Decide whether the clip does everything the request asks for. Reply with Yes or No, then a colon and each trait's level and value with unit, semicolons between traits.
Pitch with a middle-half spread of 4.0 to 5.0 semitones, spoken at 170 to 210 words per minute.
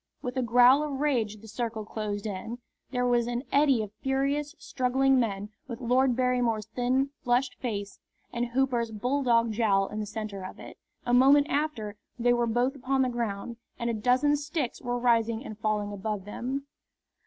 No: average, 3.3 semitones; average, 175 wpm